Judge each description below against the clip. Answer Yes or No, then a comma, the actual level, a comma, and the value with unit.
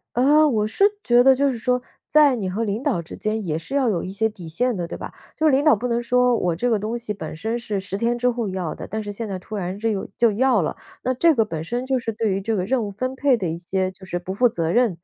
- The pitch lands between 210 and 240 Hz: Yes, high, 220 Hz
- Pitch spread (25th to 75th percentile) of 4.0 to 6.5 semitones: Yes, average, 4.7 semitones